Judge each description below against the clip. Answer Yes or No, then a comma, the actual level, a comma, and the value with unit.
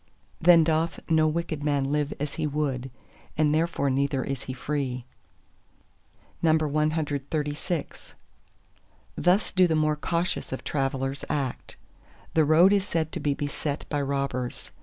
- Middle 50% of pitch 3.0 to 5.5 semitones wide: No, narrow, 2.4 semitones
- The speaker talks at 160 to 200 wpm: No, slow, 135 wpm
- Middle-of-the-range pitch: Yes, medium, 150 Hz